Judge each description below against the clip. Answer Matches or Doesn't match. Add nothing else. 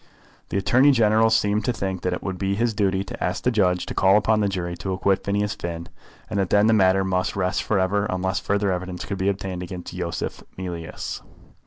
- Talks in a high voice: Doesn't match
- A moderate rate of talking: Doesn't match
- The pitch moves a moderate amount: Doesn't match